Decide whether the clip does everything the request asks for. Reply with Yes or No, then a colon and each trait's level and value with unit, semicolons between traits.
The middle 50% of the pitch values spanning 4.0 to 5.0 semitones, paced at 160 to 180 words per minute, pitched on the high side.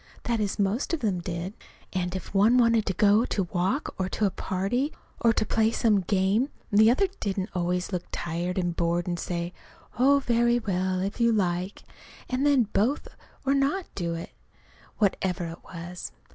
Yes: average, 4.4 semitones; average, 175 wpm; high, 195 Hz